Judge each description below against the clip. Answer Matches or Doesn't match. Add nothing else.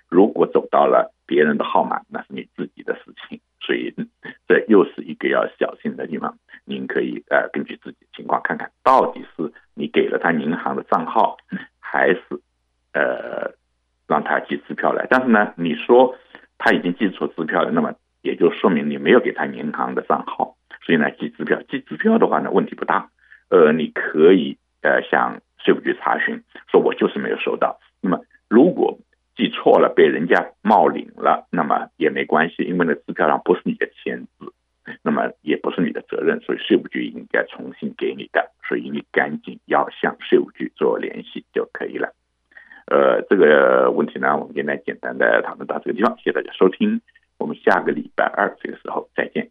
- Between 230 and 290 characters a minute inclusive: Matches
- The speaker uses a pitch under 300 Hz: Doesn't match